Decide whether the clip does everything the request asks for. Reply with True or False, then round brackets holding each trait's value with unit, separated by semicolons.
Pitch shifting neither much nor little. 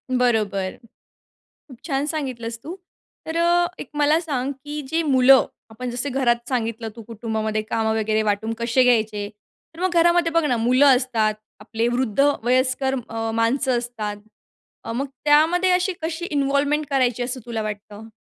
True (4.5 semitones)